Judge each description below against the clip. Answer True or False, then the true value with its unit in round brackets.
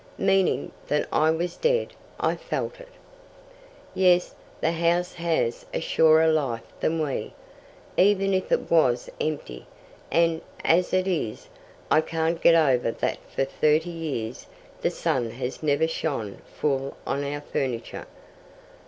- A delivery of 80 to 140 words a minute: True (135 wpm)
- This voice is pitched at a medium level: True (160 Hz)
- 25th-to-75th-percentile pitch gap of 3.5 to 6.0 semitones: True (4.1 semitones)